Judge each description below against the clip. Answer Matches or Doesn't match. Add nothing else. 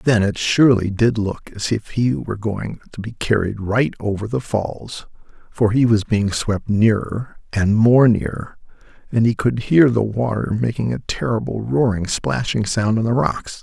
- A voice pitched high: Doesn't match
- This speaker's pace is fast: Doesn't match